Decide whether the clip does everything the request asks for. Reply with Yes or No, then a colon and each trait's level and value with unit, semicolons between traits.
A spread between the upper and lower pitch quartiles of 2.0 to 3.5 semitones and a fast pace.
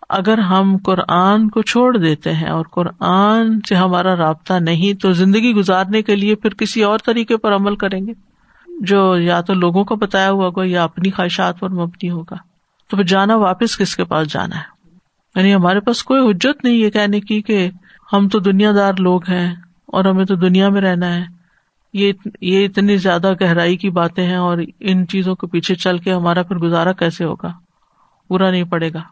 Yes: narrow, 2.5 semitones; fast, 195 wpm